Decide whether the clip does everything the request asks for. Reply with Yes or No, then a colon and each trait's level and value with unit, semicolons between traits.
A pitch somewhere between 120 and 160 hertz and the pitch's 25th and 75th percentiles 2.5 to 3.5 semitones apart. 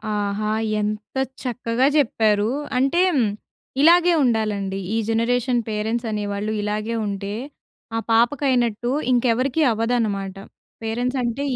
No: high, 225 Hz; average, 2.8 semitones